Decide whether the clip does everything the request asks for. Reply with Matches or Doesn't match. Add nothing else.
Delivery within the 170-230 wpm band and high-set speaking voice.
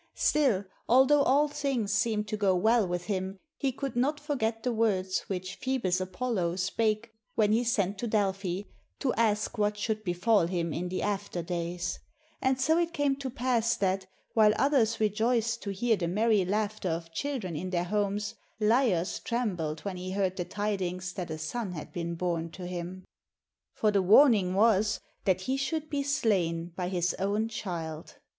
Matches